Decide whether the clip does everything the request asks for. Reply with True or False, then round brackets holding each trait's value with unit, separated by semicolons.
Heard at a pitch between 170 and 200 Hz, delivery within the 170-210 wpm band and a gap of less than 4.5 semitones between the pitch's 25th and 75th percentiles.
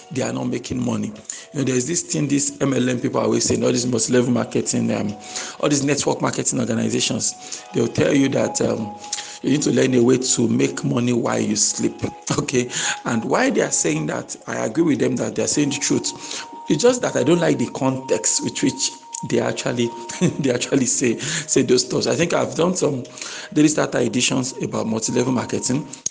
False (130 Hz; 205 wpm; 3.2 semitones)